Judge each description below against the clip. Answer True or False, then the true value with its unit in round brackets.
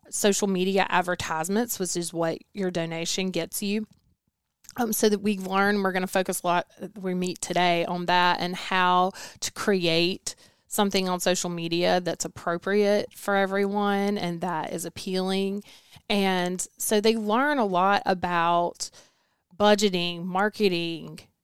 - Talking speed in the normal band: True (145 wpm)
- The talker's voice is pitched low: False (185 Hz)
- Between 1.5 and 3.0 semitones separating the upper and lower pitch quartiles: True (2.5 semitones)